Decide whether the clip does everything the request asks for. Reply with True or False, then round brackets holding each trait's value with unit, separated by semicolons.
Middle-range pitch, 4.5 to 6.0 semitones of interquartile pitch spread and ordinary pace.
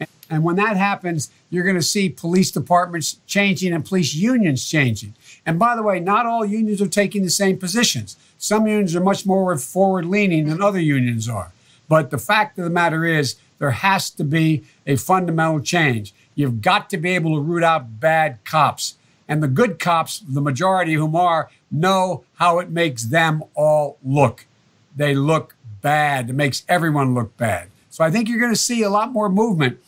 True (165 Hz; 5.0 semitones; 190 wpm)